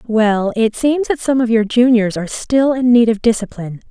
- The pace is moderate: No, fast, 215 wpm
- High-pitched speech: Yes, high, 235 Hz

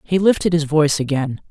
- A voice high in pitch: No, medium, 155 Hz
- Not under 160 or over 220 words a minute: Yes, average, 200 wpm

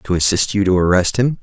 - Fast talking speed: Yes, fast, 250 wpm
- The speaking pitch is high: No, low, 100 Hz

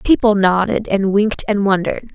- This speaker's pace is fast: No, average, 170 wpm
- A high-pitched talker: Yes, high, 205 Hz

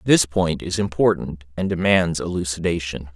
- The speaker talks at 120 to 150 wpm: Yes, slow, 135 wpm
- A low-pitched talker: Yes, very low, 85 Hz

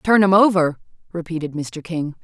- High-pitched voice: No, medium, 170 Hz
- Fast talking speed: No, average, 160 wpm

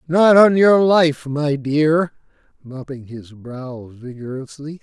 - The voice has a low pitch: No, medium, 145 Hz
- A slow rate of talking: Yes, slow, 125 wpm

